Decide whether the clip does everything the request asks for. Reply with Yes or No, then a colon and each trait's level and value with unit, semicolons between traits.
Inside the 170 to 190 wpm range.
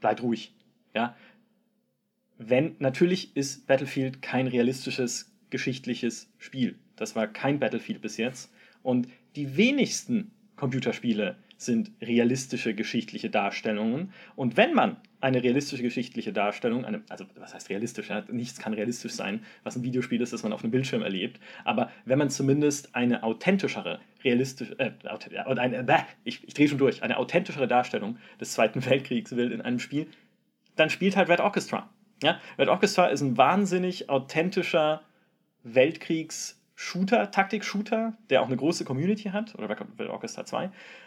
No: average, 145 wpm